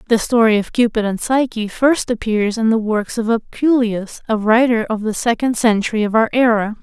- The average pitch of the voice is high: Yes, high, 225 Hz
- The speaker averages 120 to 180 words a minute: No, average, 195 wpm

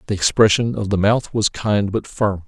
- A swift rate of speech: Yes, fast, 220 wpm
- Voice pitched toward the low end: Yes, low, 105 Hz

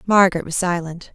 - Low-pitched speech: No, medium, 180 Hz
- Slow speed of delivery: No, average, 155 wpm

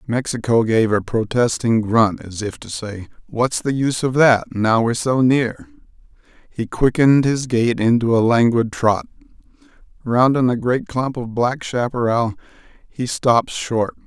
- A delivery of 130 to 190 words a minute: Yes, average, 155 wpm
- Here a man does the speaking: Yes, male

